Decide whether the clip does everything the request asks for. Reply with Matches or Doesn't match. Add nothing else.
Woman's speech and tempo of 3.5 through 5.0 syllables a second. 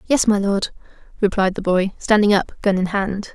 Matches